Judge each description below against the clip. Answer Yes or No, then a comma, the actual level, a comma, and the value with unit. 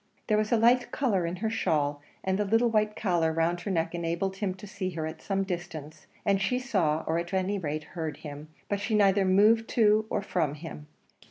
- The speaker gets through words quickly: Yes, fast, 220 wpm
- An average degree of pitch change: Yes, average, 4.3 semitones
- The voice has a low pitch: No, high, 190 Hz